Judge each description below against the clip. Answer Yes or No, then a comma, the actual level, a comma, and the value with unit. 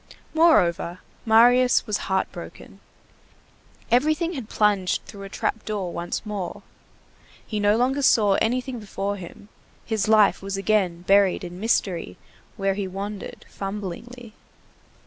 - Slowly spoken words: Yes, slow, 125 wpm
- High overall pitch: Yes, high, 205 Hz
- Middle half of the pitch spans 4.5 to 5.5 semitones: No, average, 3.3 semitones